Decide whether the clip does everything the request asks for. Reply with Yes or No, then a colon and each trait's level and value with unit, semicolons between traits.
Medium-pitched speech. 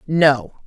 Yes: medium, 150 Hz